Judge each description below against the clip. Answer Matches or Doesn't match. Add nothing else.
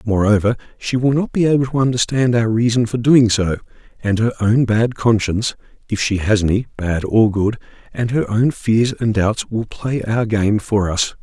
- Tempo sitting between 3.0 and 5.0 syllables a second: Matches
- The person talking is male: Matches